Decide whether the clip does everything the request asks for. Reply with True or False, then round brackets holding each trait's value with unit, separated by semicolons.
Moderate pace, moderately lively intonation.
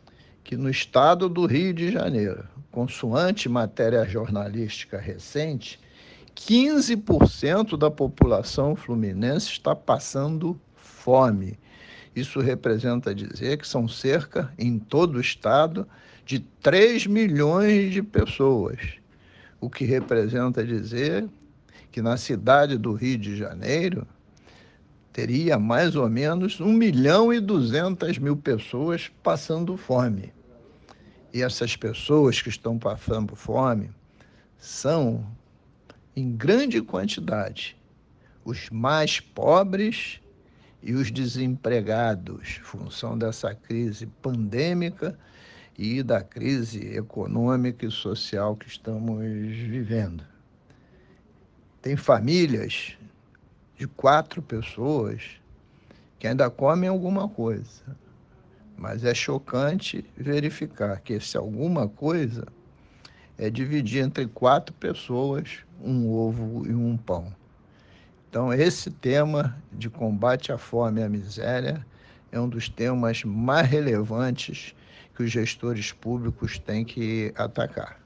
False (105 wpm; 4.5 semitones)